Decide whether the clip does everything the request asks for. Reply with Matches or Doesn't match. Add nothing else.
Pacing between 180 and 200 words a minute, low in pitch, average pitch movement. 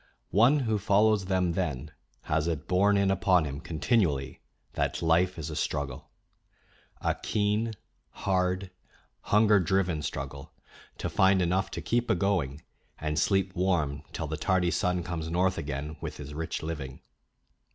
Doesn't match